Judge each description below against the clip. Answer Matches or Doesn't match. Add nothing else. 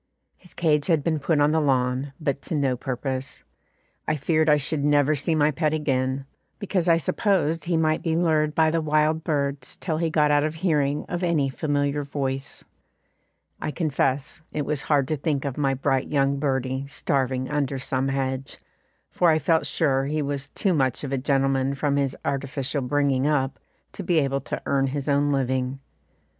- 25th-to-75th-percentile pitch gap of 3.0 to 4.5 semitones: Doesn't match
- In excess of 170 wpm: Matches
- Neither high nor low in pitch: Matches